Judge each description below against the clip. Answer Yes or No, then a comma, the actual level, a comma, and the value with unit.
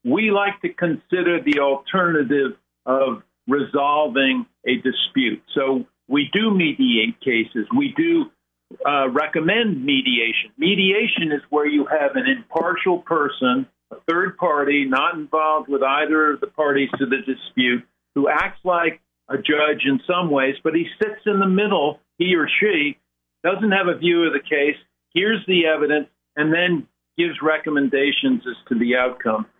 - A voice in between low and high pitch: Yes, medium, 155 Hz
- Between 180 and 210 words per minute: No, average, 155 wpm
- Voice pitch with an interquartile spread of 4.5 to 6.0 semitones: Yes, wide, 5.4 semitones